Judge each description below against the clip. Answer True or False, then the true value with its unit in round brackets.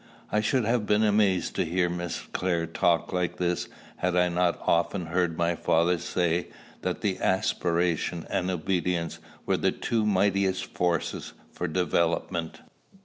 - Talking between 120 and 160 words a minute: True (145 wpm)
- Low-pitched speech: True (90 Hz)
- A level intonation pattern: True (1.7 semitones)